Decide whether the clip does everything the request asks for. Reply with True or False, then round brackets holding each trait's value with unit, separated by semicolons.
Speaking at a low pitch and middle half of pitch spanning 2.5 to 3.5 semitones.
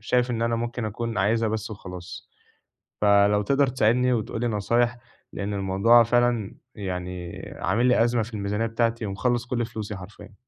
True (110 Hz; 2.9 semitones)